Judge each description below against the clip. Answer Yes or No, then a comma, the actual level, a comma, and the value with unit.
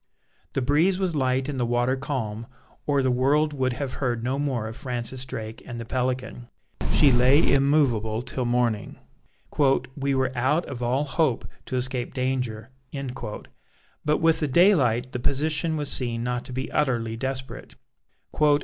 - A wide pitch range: No, average, 2.7 semitones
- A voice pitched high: No, low, 130 Hz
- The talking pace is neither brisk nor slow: Yes, average, 160 wpm